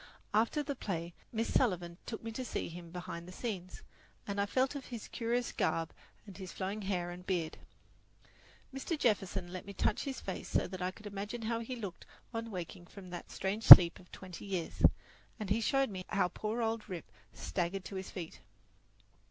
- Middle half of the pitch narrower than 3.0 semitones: No, average, 4.0 semitones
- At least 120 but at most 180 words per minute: No, average, 195 wpm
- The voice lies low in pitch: No, high, 195 Hz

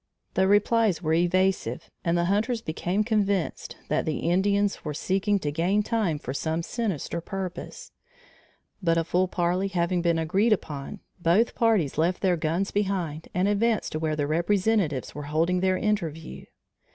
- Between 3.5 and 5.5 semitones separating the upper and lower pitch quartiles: Yes, average, 3.9 semitones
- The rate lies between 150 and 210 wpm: Yes, average, 160 wpm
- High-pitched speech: No, medium, 180 Hz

